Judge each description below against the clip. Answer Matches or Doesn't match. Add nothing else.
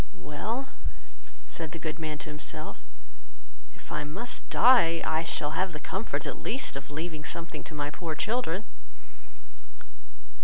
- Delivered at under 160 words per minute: Matches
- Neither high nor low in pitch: Matches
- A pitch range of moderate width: Matches